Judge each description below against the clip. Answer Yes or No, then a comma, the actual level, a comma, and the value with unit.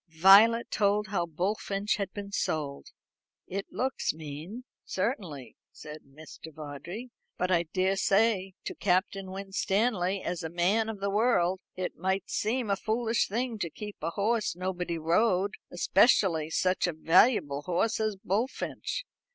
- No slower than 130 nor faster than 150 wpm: Yes, average, 140 wpm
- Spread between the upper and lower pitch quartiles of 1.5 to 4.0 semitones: Yes, average, 3.7 semitones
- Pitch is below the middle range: No, high, 190 Hz